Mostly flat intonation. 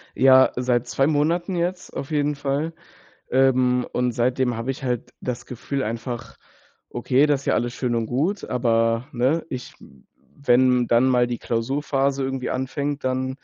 Yes: narrow, 2.3 semitones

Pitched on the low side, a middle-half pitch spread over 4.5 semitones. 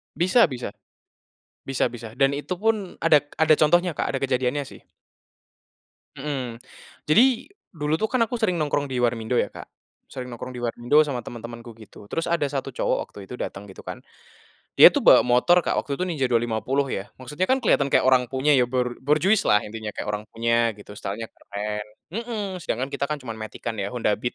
Yes: low, 130 Hz; average, 5.0 semitones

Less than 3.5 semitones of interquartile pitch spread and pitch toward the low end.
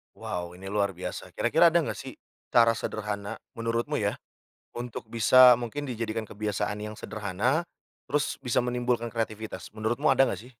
Yes: average, 2.9 semitones; low, 115 Hz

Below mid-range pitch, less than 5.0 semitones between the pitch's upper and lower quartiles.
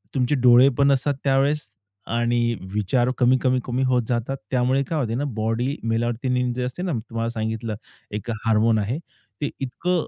Yes: low, 125 Hz; narrow, 2.6 semitones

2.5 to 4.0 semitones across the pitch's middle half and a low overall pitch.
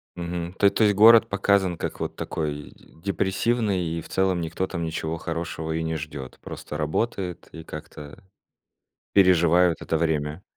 Yes: average, 3.1 semitones; very low, 85 Hz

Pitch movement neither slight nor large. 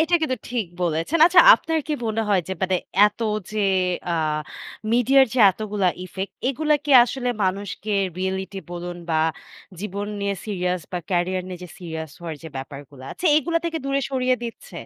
No: wide, 6.3 semitones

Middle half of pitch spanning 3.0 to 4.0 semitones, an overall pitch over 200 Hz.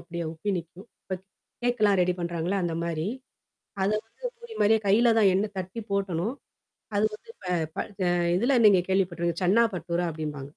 No: average, 3.7 semitones; medium, 185 Hz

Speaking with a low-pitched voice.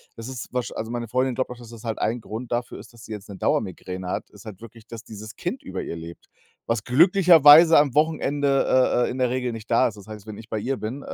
Yes: low, 115 Hz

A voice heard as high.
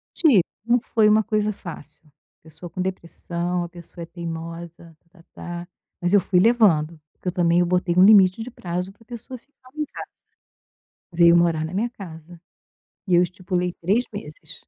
No: medium, 180 Hz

